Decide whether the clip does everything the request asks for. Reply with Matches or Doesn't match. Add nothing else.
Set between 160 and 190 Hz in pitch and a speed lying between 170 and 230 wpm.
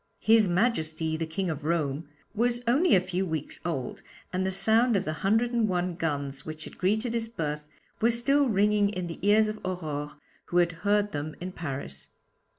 Matches